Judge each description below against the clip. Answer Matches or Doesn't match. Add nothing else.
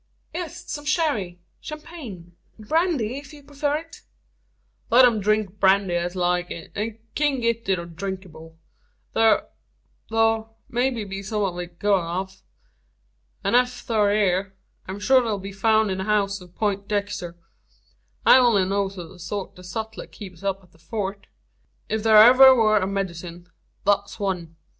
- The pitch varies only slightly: Doesn't match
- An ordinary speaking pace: Matches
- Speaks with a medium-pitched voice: Doesn't match